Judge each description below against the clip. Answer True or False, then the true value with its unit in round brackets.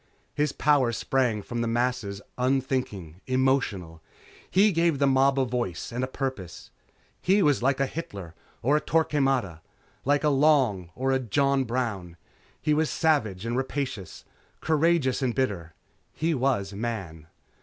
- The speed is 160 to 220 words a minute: False (145 wpm)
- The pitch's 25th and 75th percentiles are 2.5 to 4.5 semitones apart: False (5.0 semitones)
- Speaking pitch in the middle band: False (130 Hz)